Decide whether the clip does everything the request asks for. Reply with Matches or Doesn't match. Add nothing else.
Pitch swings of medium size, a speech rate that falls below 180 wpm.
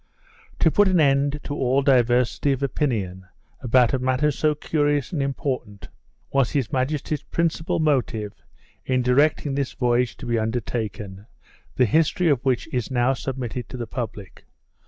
Matches